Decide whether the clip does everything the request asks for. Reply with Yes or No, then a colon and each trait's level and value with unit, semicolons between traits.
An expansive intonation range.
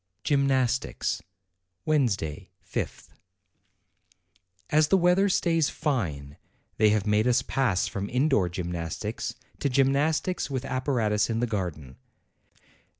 Yes: wide, 6.2 semitones